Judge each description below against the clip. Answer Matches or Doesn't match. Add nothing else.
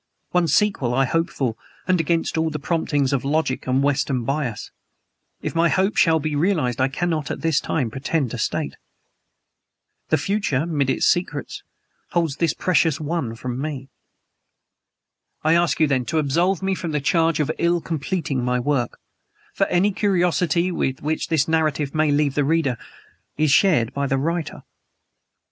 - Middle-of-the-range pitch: Matches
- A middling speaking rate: Matches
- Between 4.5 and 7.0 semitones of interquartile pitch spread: Doesn't match